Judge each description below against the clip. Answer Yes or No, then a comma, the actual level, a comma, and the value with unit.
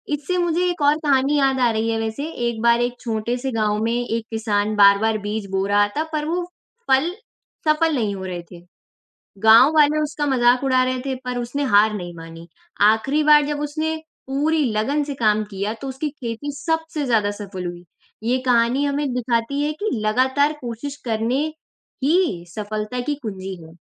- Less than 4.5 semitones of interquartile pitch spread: No, average, 5.2 semitones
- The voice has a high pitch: Yes, high, 245 Hz